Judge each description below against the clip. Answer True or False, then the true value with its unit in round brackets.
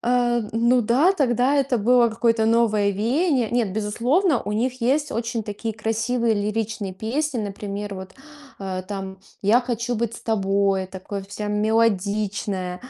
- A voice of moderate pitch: False (225 Hz)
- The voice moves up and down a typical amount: True (3.1 semitones)